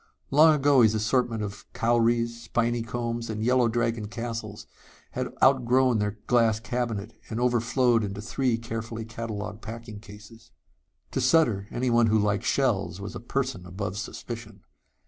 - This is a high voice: No, low, 115 Hz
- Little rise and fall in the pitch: Yes, narrow, 2.1 semitones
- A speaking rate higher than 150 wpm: No, average, 145 wpm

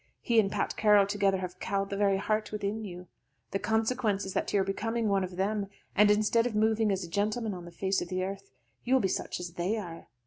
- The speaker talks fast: Yes, fast, 245 wpm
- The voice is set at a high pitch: Yes, high, 200 Hz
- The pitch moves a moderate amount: No, narrow, 2.1 semitones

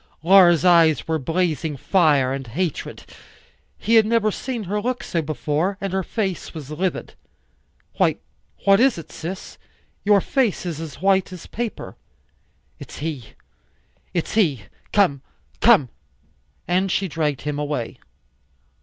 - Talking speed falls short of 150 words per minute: Yes, slow, 135 wpm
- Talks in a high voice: No, medium, 175 Hz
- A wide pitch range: No, average, 4.6 semitones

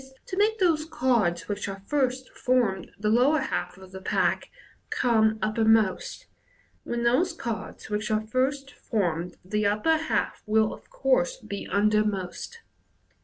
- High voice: Yes, high, 220 Hz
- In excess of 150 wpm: No, average, 140 wpm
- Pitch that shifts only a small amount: No, wide, 5.4 semitones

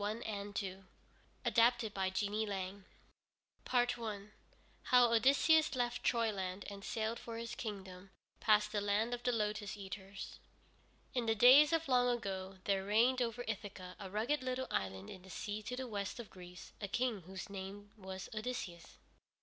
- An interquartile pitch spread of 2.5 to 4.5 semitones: Yes, average, 3.6 semitones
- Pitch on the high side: Yes, high, 210 Hz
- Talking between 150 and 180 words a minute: Yes, average, 155 wpm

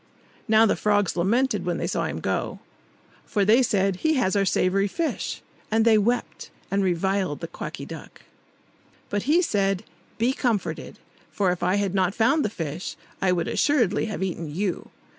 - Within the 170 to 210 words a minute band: Yes, average, 175 wpm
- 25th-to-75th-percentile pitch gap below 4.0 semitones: Yes, average, 3.4 semitones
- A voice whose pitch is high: Yes, high, 200 Hz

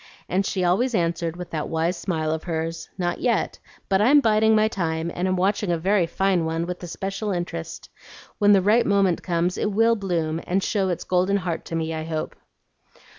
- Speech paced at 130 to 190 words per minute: No, average, 200 wpm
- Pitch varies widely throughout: No, average, 3.3 semitones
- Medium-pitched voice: Yes, medium, 180 Hz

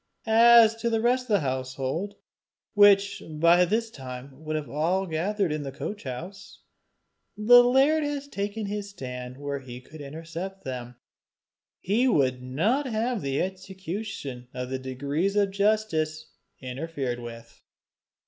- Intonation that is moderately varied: No, wide, 7.8 semitones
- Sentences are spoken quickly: No, average, 145 wpm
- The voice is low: No, medium, 170 Hz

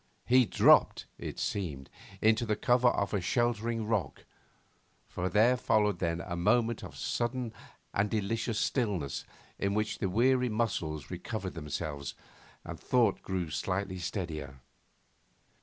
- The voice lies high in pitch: No, low, 105 Hz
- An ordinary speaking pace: No, slow, 130 wpm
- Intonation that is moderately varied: Yes, average, 4.9 semitones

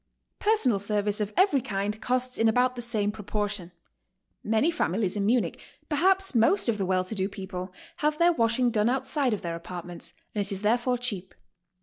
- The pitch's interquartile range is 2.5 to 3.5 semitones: No, average, 4.2 semitones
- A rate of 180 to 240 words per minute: Yes, average, 190 wpm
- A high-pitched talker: Yes, high, 220 Hz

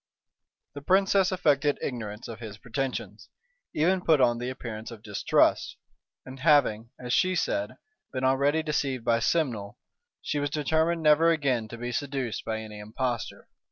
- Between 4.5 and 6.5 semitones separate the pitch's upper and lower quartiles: Yes, average, 4.8 semitones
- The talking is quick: No, average, 155 wpm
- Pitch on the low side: Yes, low, 130 Hz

